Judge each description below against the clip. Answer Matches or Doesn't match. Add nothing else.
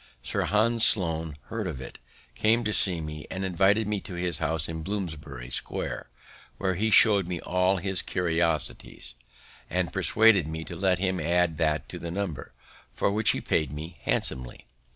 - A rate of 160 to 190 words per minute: Matches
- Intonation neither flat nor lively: Matches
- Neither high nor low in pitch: Doesn't match